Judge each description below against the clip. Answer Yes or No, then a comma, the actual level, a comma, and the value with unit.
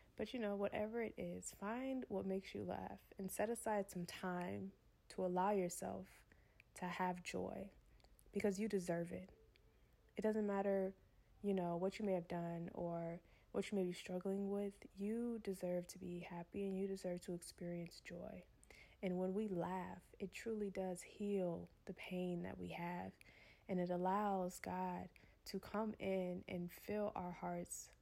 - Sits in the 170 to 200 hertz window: Yes, medium, 185 Hz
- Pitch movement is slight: Yes, narrow, 2.2 semitones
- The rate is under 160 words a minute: No, average, 165 wpm